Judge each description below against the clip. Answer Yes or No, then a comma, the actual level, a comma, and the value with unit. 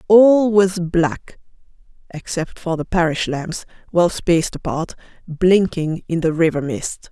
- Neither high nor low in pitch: Yes, medium, 170 Hz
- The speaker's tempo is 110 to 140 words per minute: Yes, slow, 135 wpm